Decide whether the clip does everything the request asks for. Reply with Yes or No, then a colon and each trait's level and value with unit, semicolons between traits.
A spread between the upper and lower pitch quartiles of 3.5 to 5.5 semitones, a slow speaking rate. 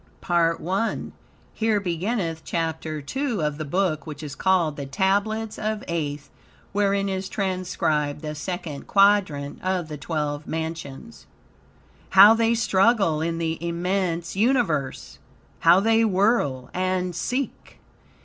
Yes: average, 4.4 semitones; slow, 125 wpm